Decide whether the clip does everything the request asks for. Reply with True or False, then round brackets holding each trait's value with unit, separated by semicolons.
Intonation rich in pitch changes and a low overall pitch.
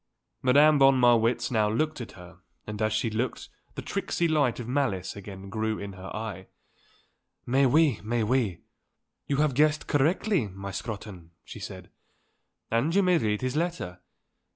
True (5.7 semitones; 115 Hz)